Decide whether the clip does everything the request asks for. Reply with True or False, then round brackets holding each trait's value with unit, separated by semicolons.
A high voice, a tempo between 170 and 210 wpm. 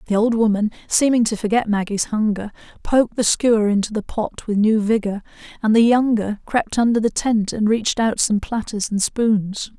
True (220 Hz; 190 wpm)